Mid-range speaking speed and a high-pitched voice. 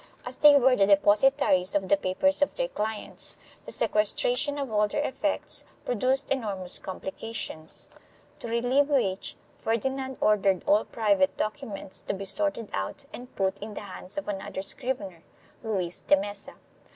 Yes: average, 160 wpm; high, 215 Hz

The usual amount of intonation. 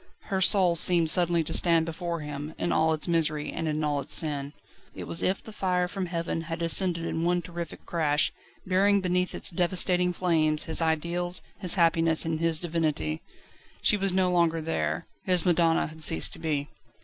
No: narrow, 2.2 semitones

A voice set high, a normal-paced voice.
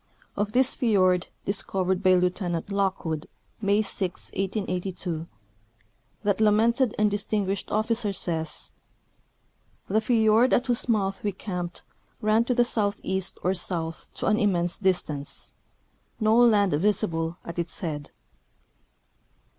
No: high, 195 Hz; slow, 125 wpm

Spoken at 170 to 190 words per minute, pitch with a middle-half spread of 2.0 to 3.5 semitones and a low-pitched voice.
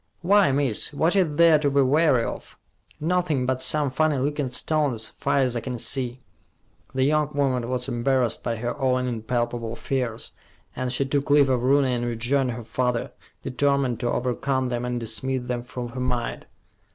Yes: average, 175 wpm; average, 2.7 semitones; low, 130 Hz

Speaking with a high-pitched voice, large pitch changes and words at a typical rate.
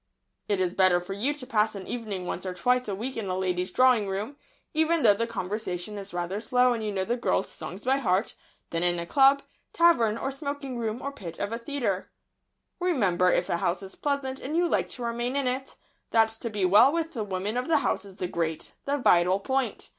No: high, 220 Hz; wide, 5.8 semitones; fast, 230 wpm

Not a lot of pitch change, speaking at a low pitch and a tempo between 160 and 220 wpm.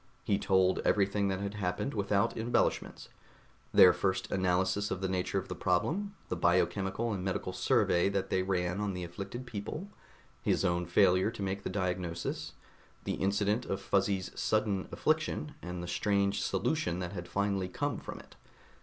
Yes: narrow, 1.9 semitones; very low, 95 Hz; average, 165 wpm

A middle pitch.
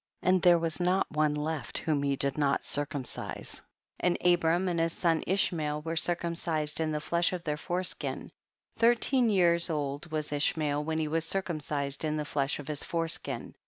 Yes: medium, 160 Hz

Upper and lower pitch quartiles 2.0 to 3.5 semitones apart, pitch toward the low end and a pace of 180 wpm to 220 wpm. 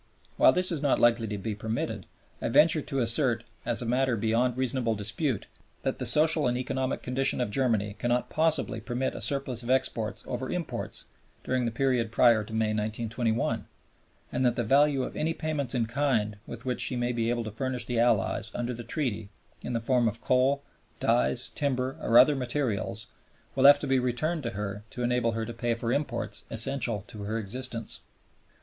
Yes: average, 2.7 semitones; low, 120 Hz; average, 195 wpm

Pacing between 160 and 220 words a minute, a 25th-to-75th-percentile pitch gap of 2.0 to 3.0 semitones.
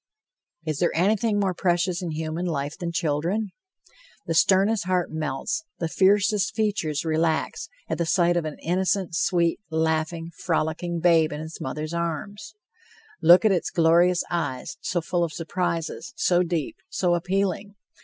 No: average, 150 wpm; narrow, 2.6 semitones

